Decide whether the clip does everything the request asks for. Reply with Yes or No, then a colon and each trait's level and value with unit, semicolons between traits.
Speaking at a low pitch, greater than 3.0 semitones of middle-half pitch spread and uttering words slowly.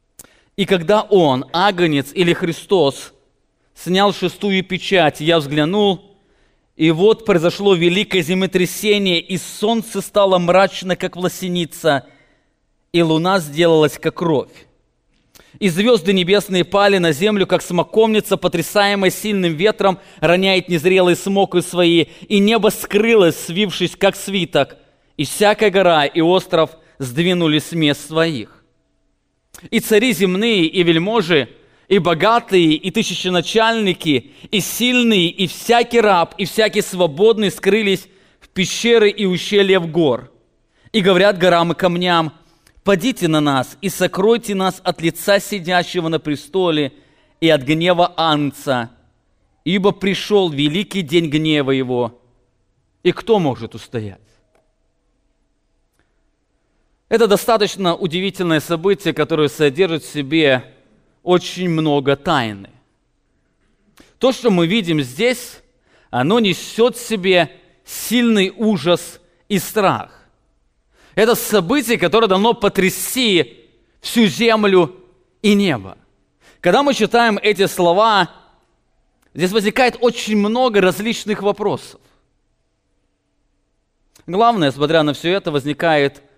No: medium, 180 Hz; average, 4.1 semitones; slow, 110 wpm